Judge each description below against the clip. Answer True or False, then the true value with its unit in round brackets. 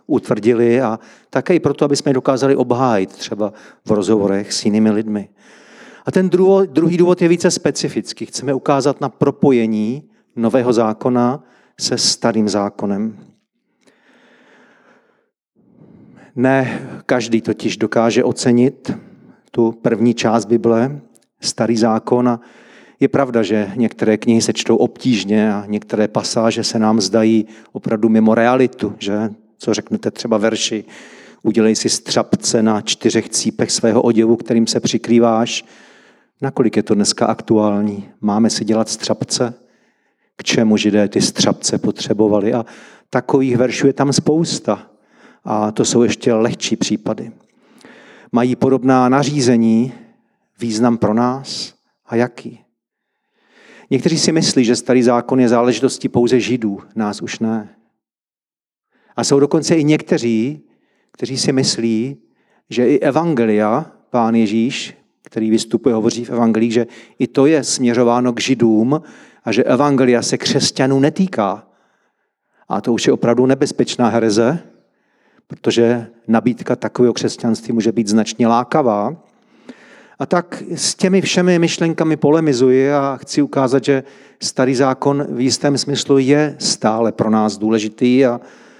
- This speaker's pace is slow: False (130 wpm)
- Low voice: True (120 Hz)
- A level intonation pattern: False (3.5 semitones)